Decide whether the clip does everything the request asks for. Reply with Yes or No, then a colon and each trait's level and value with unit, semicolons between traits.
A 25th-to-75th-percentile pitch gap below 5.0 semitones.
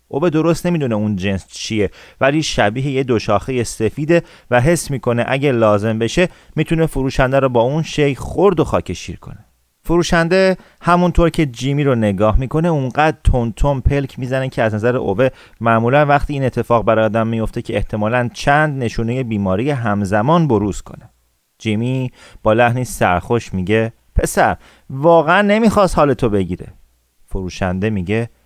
No: wide, 5.5 semitones